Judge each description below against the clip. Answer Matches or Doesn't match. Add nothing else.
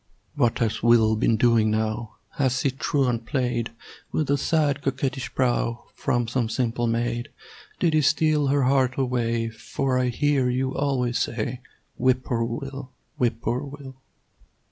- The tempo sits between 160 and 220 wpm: Doesn't match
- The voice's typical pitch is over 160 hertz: Doesn't match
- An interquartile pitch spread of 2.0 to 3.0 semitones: Matches